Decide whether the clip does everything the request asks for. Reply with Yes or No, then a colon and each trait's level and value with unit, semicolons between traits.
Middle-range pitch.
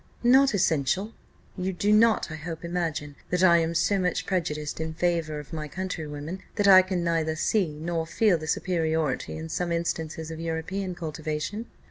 Yes: medium, 170 Hz